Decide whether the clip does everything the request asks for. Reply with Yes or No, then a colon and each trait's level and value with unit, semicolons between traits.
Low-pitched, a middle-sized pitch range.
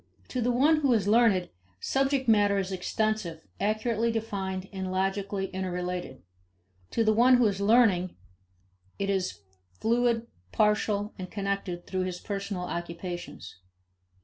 No: high, 200 Hz; average, 3.4 semitones